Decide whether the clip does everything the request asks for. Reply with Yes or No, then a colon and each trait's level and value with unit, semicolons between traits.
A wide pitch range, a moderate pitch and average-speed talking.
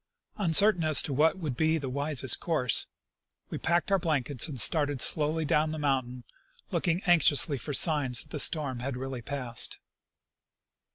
No: average, 3.5 semitones; medium, 150 Hz; average, 170 wpm